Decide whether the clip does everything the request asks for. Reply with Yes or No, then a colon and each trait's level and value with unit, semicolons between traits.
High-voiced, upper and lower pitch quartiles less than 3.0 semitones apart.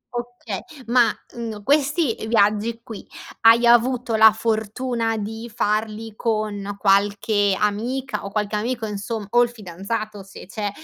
Yes: high, 220 Hz; narrow, 2.4 semitones